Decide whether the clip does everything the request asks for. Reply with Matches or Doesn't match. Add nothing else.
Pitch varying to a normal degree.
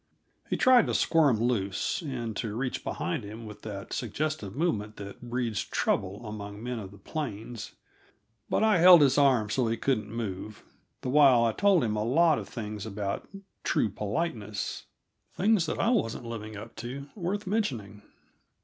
Doesn't match